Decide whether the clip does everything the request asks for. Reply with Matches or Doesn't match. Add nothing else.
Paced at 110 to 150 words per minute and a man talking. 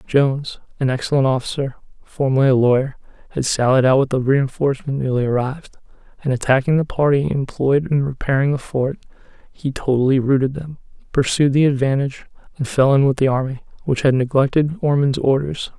Doesn't match